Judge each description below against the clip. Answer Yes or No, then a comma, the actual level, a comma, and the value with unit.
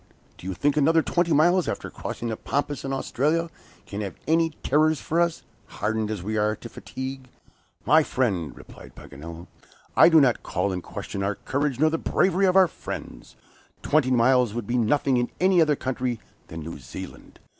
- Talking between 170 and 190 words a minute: Yes, average, 185 wpm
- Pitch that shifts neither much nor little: No, wide, 6.5 semitones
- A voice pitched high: No, low, 130 Hz